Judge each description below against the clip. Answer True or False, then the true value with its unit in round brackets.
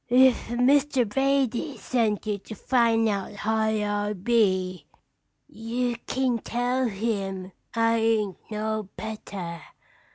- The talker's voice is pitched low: False (220 Hz)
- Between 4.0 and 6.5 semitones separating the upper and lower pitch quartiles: False (3.0 semitones)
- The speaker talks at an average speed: False (110 wpm)